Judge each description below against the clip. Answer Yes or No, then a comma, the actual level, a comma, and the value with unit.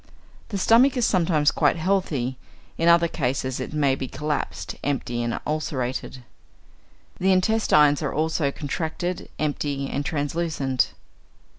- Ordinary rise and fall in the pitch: Yes, average, 3.8 semitones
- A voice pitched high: No, medium, 150 Hz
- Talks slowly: Yes, slow, 125 wpm